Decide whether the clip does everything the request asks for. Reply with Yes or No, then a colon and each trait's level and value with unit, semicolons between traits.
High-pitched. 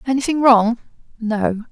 Yes: high, 235 Hz